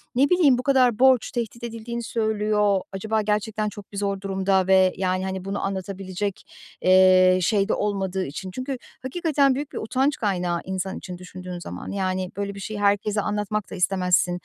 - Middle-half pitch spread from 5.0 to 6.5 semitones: No, average, 2.8 semitones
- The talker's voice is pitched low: No, high, 200 Hz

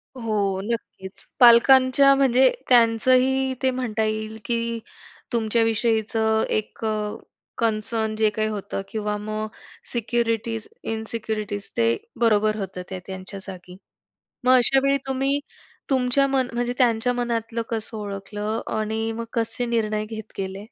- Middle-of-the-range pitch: No, high, 225 Hz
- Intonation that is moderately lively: No, narrow, 2.2 semitones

